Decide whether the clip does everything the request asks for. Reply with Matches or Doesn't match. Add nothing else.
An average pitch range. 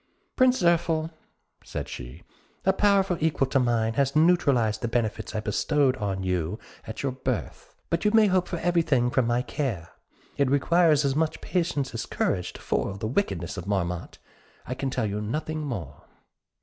Doesn't match